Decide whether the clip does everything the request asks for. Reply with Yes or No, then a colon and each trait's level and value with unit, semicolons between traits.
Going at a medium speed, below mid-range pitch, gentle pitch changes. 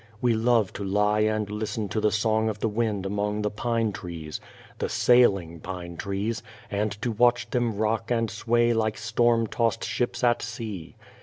Yes: average, 175 wpm; low, 110 Hz; narrow, 2.2 semitones